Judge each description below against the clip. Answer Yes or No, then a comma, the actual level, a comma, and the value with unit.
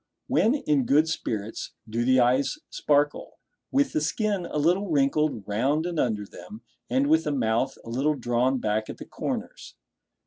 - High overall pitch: No, medium, 140 Hz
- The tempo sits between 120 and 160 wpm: No, average, 170 wpm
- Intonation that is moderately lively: No, wide, 5.7 semitones